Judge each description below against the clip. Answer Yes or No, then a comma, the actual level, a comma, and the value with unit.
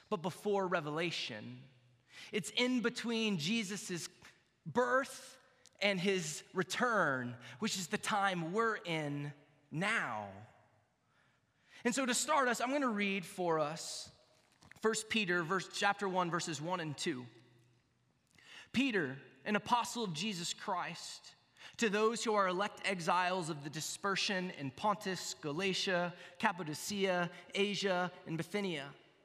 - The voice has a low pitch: No, medium, 185 Hz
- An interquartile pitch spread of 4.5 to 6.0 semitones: Yes, wide, 5.4 semitones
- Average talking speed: No, slow, 125 wpm